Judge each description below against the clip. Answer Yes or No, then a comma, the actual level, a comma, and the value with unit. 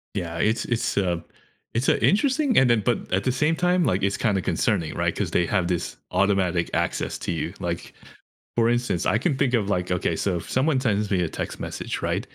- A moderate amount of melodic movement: No, wide, 6.3 semitones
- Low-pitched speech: Yes, low, 105 Hz